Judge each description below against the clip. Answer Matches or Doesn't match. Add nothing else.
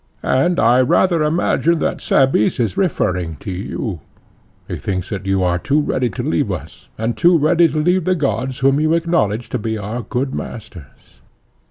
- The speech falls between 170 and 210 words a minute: Matches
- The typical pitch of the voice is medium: Doesn't match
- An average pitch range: Doesn't match